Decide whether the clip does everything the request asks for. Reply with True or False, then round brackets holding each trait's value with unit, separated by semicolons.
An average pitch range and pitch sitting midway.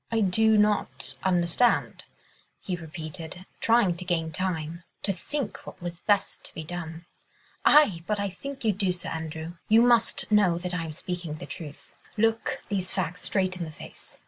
True (4.1 semitones; 180 Hz)